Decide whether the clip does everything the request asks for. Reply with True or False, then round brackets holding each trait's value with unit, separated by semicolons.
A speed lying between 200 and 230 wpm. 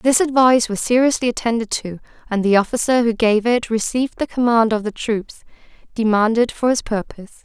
False (175 wpm)